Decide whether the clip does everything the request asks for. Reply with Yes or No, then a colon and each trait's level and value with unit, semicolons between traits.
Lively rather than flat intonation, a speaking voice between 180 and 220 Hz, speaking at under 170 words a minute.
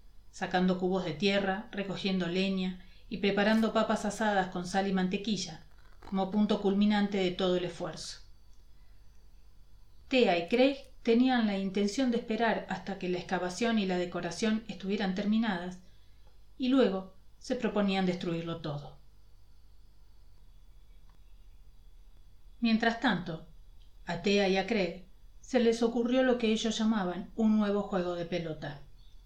Yes: wide, 6.7 semitones; high, 190 Hz; average, 130 wpm